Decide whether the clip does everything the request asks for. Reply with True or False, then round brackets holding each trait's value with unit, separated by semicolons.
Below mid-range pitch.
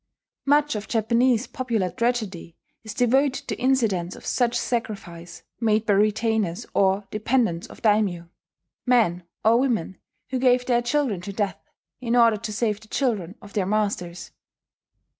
False (220 Hz)